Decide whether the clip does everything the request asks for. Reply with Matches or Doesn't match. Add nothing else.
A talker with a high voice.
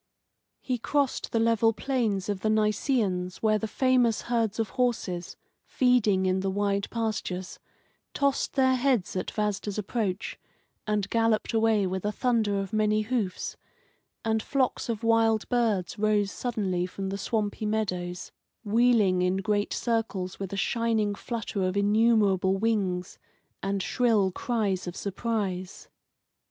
Matches